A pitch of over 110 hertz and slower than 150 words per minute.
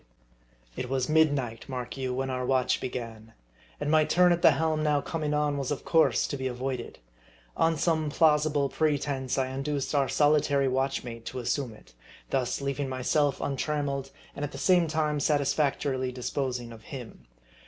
No: medium, 140 Hz; average, 165 wpm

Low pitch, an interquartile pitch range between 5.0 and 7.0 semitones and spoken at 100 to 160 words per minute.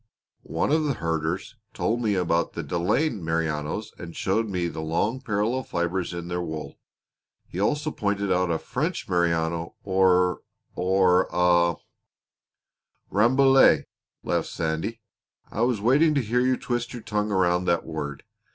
Yes: very low, 95 Hz; wide, 5.4 semitones; average, 150 wpm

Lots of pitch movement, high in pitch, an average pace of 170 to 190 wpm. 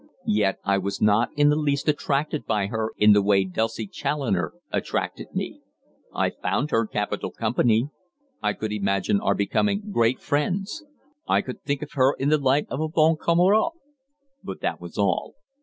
No: wide, 6.3 semitones; low, 130 Hz; average, 175 wpm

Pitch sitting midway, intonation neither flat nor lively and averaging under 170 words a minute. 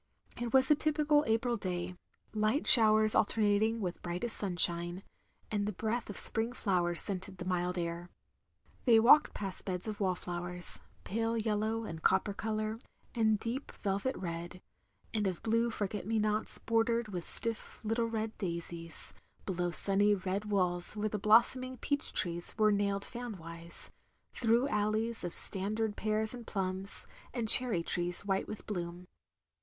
No: high, 210 Hz; average, 3.7 semitones; average, 155 wpm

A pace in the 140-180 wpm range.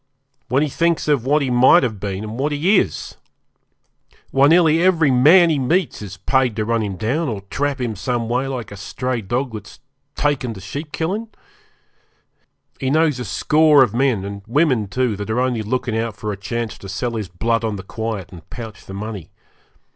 No: average, 200 wpm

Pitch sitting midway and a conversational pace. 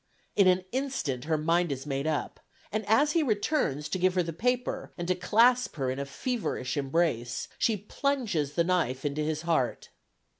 Yes: medium, 170 Hz; average, 185 wpm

